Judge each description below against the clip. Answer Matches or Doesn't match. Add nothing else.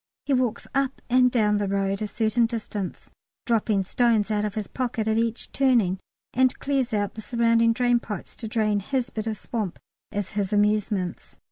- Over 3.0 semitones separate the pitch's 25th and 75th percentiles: Doesn't match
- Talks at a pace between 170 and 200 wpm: Matches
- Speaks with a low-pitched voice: Doesn't match